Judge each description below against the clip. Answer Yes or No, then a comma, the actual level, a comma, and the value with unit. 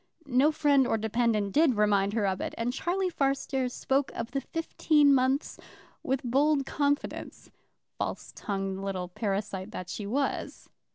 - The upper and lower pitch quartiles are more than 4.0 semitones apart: Yes, wide, 5.5 semitones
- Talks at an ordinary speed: Yes, average, 150 wpm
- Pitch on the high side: Yes, very high, 250 Hz